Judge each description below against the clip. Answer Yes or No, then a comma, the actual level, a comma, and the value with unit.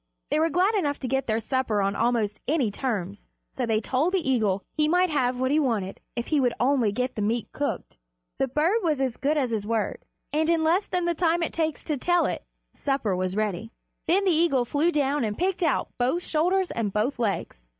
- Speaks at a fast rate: Yes, fast, 220 wpm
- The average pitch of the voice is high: Yes, very high, 270 Hz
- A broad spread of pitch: Yes, wide, 6.1 semitones